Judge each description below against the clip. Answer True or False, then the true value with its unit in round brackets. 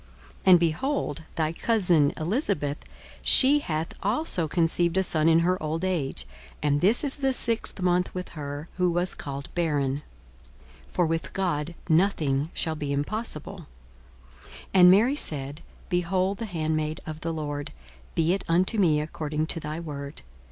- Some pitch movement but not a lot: True (3.5 semitones)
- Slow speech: False (160 wpm)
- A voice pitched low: False (165 Hz)